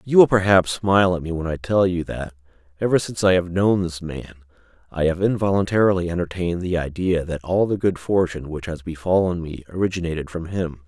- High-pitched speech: No, very low, 90 Hz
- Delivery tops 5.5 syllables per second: Yes, 6.0 syllables/s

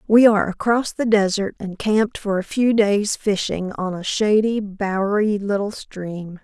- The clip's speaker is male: No, female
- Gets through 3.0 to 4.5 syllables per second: Yes, 4.3 syllables/s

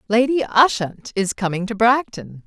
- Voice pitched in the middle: No, high, 220 Hz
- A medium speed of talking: Yes, average, 145 wpm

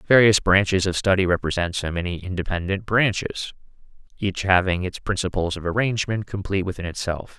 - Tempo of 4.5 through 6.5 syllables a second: Yes, 5.8 syllables/s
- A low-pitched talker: Yes, very low, 95 Hz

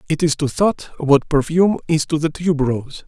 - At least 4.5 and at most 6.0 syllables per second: Yes, 5.5 syllables/s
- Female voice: No, male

